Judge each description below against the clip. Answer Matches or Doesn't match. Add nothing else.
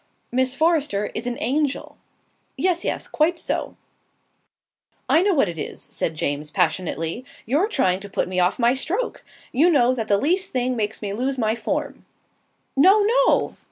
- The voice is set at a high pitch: Matches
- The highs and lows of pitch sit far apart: Matches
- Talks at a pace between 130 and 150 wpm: Doesn't match